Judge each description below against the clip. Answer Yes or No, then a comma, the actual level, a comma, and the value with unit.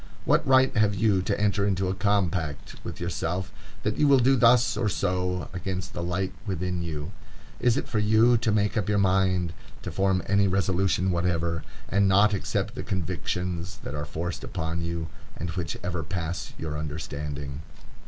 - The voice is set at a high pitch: No, very low, 95 Hz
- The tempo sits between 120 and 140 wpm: No, average, 170 wpm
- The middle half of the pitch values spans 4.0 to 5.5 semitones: No, average, 3.2 semitones